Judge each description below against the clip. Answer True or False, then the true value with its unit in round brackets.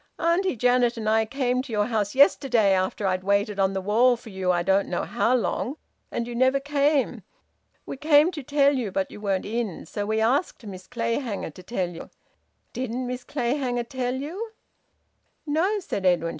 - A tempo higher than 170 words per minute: True (185 wpm)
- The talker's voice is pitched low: False (240 Hz)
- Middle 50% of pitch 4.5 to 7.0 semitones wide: True (5.1 semitones)